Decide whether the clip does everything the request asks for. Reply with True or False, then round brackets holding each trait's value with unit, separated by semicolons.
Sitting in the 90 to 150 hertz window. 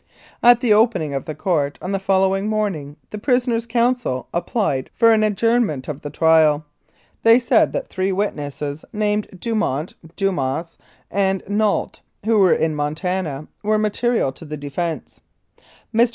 False (195 Hz)